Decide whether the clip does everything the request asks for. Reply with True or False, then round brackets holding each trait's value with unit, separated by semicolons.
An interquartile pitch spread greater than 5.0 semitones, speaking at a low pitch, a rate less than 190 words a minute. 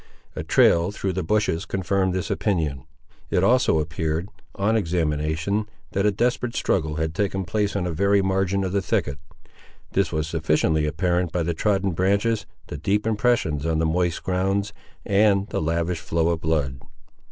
False (3.8 semitones; 90 Hz; 165 wpm)